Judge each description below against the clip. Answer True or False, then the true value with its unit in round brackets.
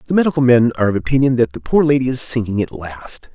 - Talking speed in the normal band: False (250 wpm)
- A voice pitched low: True (120 Hz)